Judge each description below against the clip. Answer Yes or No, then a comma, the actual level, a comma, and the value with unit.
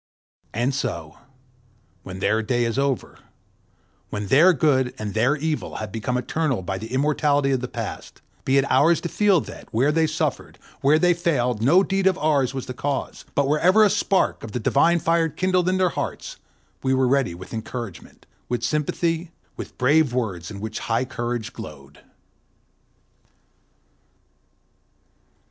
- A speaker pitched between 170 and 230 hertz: No, low, 135 Hz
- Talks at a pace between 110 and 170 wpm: Yes, average, 160 wpm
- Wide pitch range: Yes, wide, 5.7 semitones